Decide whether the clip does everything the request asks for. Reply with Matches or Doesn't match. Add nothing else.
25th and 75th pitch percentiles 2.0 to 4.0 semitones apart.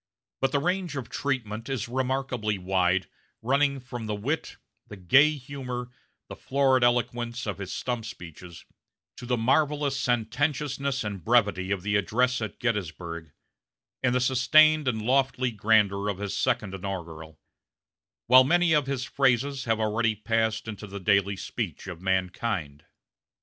Doesn't match